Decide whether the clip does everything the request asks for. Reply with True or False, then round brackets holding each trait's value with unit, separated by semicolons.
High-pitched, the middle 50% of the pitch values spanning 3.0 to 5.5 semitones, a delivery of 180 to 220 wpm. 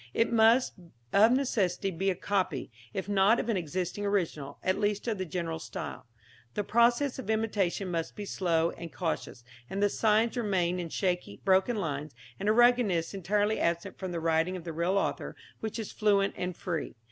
True (195 Hz; 3.9 semitones; 185 wpm)